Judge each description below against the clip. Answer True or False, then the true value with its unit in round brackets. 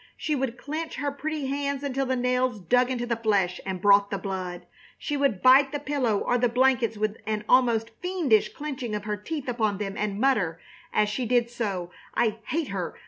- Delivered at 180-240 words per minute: True (200 wpm)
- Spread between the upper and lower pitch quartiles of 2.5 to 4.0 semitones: False (4.6 semitones)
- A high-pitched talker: True (240 Hz)